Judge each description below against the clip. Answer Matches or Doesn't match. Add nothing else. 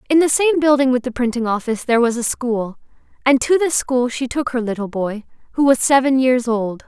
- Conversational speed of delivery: Doesn't match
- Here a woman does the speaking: Matches